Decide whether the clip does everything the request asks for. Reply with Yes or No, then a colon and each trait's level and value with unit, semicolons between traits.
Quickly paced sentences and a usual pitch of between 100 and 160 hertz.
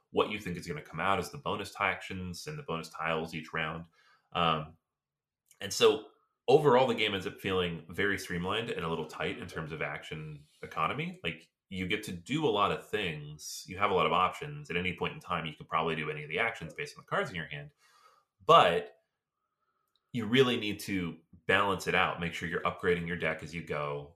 No: fast, 225 wpm; very low, 90 Hz